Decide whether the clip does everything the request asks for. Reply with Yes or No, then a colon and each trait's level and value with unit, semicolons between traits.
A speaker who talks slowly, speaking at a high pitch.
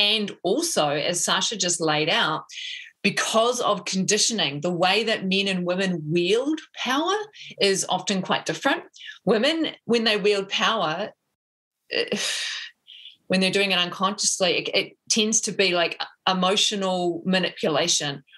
Yes: slow, 130 wpm; high, 200 Hz